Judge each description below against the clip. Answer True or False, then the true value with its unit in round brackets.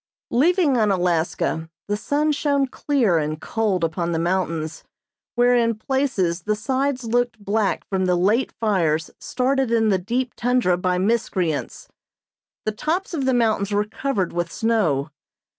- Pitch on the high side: True (215 Hz)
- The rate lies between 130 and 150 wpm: True (145 wpm)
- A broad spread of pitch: True (5.8 semitones)